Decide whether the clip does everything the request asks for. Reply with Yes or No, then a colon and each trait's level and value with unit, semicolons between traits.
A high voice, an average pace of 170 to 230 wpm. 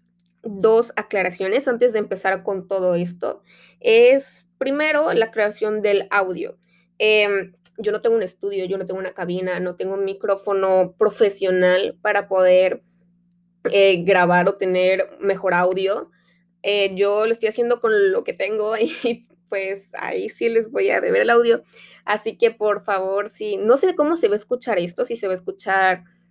Yes: high, 200 Hz; average, 175 wpm